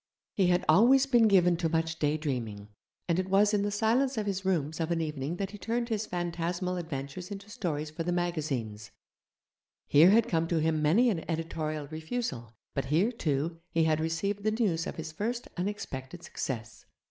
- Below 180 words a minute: No, average, 185 wpm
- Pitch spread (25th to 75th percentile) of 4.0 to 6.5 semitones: Yes, average, 4.7 semitones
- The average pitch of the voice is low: No, medium, 170 Hz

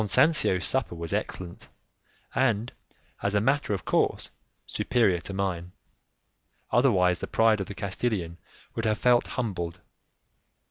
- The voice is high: No, low, 100 Hz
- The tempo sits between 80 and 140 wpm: Yes, slow, 135 wpm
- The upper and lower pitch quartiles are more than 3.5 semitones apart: Yes, average, 4.9 semitones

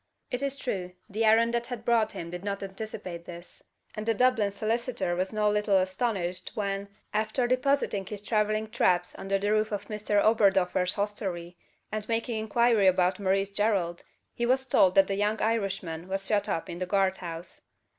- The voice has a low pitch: No, high, 205 Hz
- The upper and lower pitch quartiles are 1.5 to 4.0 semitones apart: Yes, average, 2.8 semitones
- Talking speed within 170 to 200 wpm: Yes, average, 180 wpm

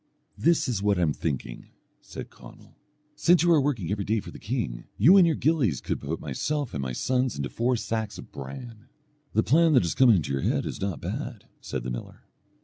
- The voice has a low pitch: Yes, low, 110 Hz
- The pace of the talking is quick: Yes, fast, 220 wpm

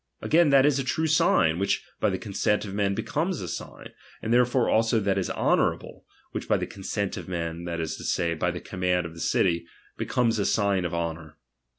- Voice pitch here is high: No, very low, 95 Hz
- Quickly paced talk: Yes, fast, 215 wpm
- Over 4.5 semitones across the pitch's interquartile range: Yes, average, 5.2 semitones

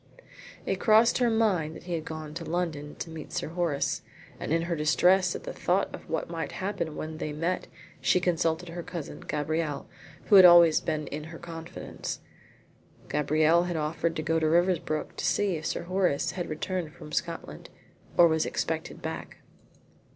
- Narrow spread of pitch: Yes, narrow, 2.3 semitones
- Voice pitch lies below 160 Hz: No, medium, 165 Hz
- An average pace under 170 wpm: No, average, 180 wpm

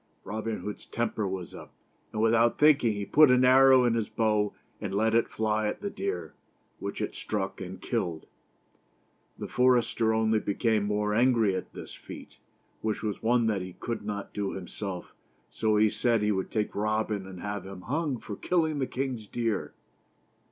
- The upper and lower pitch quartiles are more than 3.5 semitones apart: No, narrow, 2.6 semitones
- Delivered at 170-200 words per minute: Yes, average, 180 wpm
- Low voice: Yes, low, 110 Hz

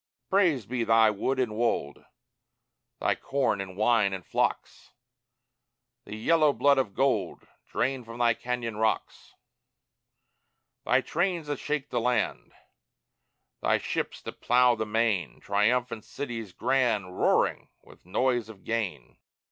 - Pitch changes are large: No, average, 3.5 semitones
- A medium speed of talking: No, slow, 130 wpm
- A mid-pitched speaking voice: No, low, 115 Hz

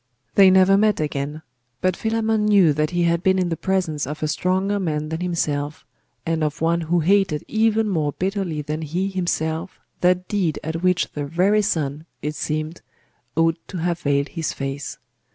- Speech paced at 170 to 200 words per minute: Yes, average, 180 wpm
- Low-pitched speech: No, medium, 170 Hz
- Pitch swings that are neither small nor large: Yes, average, 3.7 semitones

